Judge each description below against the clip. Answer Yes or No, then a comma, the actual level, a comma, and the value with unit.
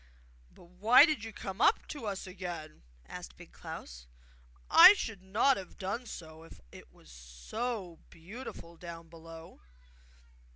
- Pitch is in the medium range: Yes, medium, 180 Hz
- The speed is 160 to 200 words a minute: No, average, 140 wpm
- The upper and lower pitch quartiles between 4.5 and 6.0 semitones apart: Yes, average, 5.2 semitones